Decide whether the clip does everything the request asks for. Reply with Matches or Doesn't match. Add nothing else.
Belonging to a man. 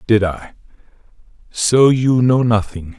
Matches